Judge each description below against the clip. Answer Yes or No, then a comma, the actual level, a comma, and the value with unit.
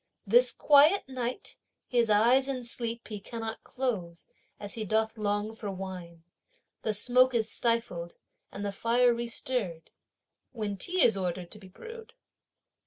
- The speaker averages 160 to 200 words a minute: No, average, 145 wpm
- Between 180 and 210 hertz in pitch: No, high, 225 Hz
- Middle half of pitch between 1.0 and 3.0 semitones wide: No, average, 3.7 semitones